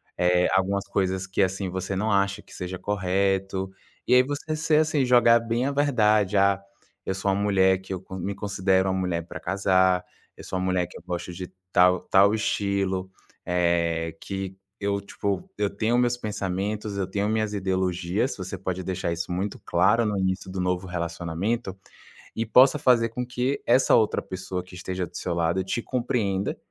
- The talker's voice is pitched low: Yes, very low, 95 Hz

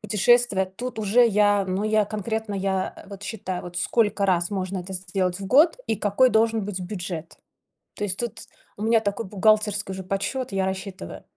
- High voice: Yes, high, 200 Hz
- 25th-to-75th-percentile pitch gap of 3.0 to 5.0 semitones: No, narrow, 2.5 semitones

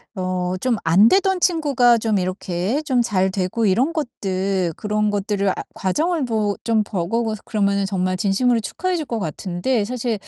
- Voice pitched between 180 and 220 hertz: Yes, high, 210 Hz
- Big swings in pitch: No, average, 4.5 semitones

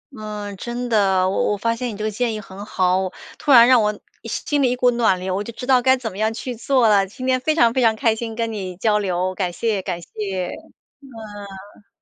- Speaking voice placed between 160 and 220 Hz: Yes, high, 215 Hz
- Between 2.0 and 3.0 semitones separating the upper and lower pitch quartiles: No, average, 3.6 semitones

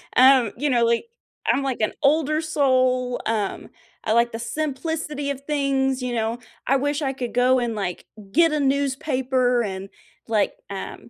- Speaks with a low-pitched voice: No, very high, 260 Hz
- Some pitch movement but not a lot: Yes, average, 3.2 semitones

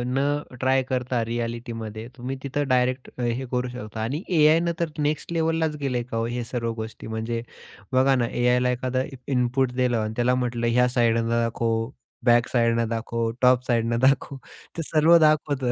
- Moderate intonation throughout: No, narrow, 2.3 semitones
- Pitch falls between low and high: No, low, 125 Hz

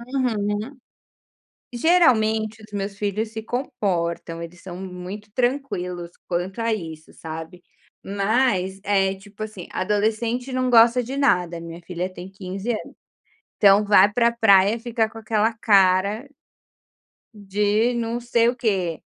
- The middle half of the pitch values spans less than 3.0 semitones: No, average, 3.6 semitones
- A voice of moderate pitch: No, high, 210 Hz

